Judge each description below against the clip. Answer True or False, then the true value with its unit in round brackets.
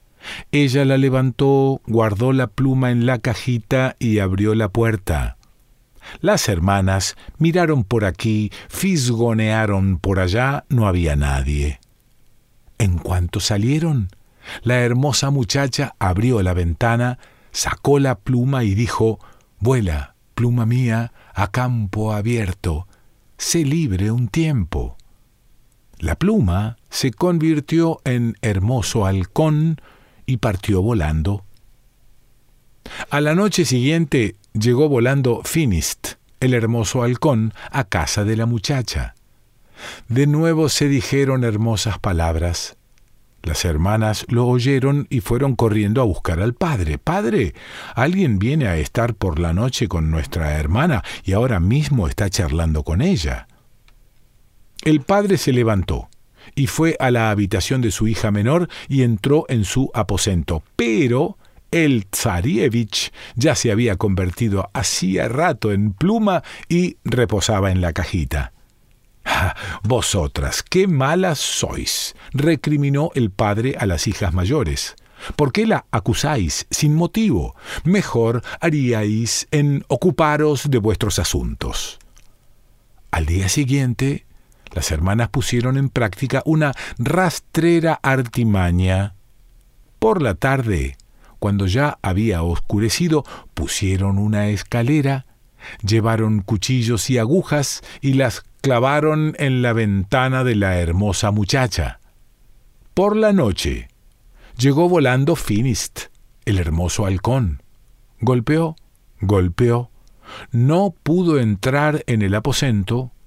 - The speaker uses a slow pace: True (115 wpm)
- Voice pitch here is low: True (120 Hz)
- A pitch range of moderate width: True (4.9 semitones)